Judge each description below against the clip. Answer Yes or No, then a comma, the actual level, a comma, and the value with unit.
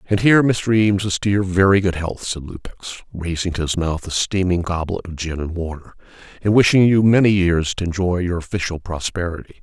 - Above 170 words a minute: Yes, fast, 205 wpm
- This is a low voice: Yes, very low, 90 Hz